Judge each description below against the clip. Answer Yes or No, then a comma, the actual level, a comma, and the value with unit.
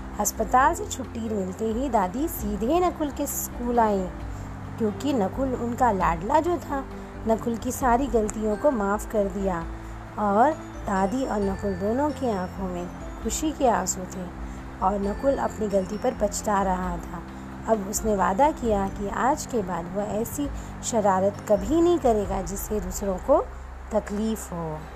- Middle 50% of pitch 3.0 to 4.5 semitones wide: Yes, average, 4.1 semitones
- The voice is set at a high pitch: Yes, high, 210 Hz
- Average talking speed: Yes, average, 155 wpm